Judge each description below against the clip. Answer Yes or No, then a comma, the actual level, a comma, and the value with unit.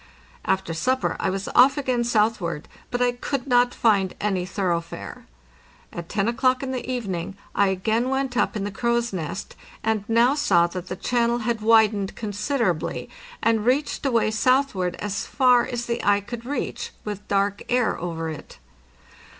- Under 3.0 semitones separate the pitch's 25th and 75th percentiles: No, average, 4.2 semitones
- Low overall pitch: No, high, 220 Hz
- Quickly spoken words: No, average, 165 wpm